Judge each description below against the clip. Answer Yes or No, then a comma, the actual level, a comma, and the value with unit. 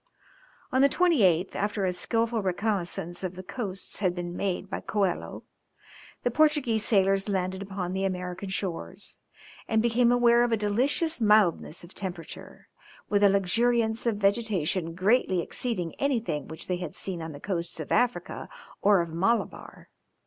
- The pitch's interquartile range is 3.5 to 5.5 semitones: Yes, average, 4.2 semitones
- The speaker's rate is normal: Yes, average, 155 wpm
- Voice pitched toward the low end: No, high, 195 Hz